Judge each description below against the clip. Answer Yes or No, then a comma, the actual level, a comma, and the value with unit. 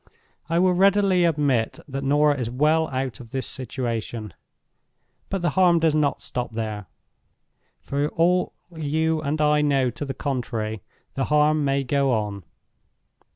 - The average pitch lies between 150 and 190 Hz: No, medium, 140 Hz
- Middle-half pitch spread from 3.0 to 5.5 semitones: Yes, average, 4.2 semitones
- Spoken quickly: No, average, 150 wpm